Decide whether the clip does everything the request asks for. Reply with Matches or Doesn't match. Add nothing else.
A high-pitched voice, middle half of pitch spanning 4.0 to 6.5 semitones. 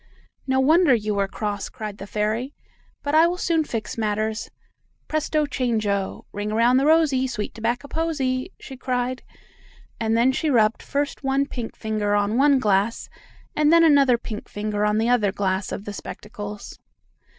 Matches